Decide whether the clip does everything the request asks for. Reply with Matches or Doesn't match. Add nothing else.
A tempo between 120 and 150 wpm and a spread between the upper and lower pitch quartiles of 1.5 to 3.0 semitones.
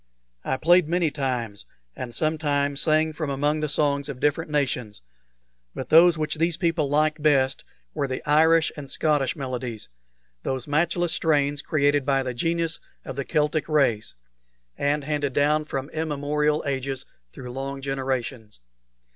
Matches